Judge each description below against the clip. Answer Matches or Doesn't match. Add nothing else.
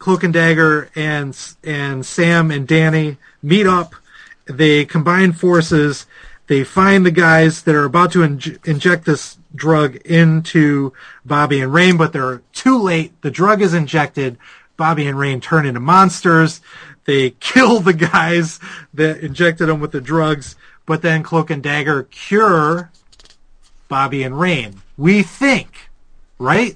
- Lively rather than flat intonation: Doesn't match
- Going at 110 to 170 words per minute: Matches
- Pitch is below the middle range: Doesn't match